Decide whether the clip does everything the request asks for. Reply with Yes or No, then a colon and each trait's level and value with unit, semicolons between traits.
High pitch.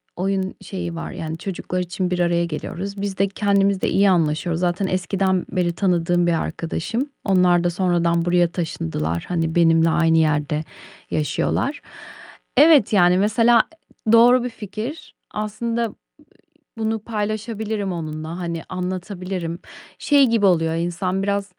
No: medium, 180 Hz